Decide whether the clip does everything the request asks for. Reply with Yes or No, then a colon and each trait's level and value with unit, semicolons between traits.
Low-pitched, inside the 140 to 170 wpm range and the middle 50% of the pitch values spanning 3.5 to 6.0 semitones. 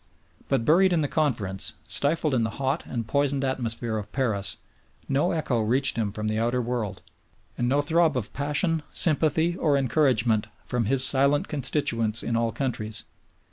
Yes: low, 130 Hz; average, 165 wpm; average, 4.2 semitones